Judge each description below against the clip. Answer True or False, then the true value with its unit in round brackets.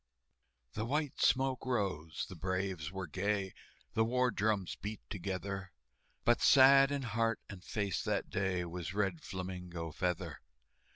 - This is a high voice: False (100 Hz)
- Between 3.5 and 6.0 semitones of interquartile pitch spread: True (3.9 semitones)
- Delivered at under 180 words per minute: True (135 wpm)